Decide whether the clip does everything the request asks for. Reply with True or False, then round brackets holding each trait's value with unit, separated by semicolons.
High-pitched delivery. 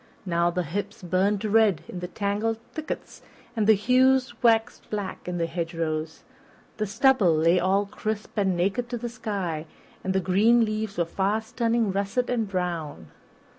True (200 Hz)